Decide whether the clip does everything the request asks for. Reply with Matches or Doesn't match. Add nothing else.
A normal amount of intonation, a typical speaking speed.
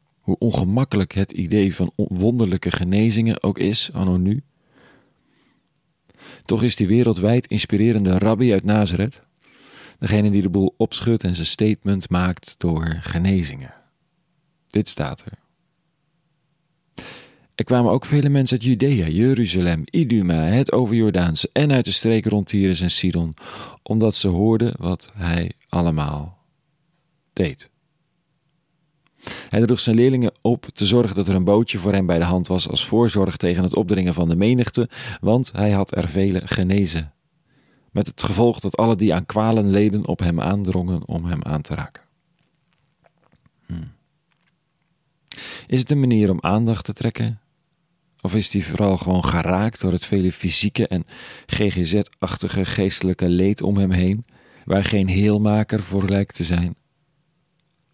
Doesn't match